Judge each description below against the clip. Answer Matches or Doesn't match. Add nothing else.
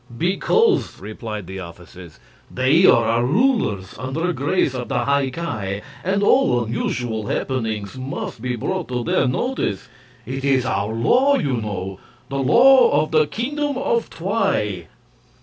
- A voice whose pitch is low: Matches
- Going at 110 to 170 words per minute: Matches